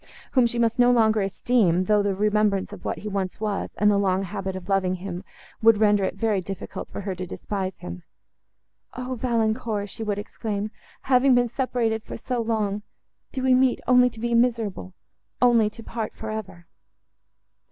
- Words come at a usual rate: Yes, average, 175 wpm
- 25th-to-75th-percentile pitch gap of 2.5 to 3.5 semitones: Yes, average, 3.2 semitones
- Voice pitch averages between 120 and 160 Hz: No, high, 215 Hz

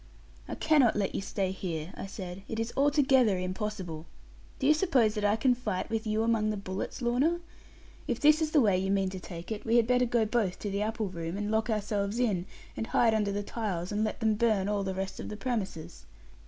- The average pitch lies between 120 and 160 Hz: No, high, 210 Hz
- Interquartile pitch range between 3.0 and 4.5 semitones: Yes, average, 3.5 semitones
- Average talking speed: No, fast, 230 wpm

